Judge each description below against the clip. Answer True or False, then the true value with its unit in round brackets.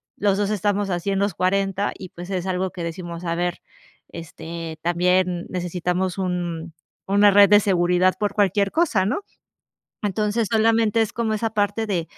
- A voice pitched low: False (190 Hz)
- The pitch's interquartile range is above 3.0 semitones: False (2.7 semitones)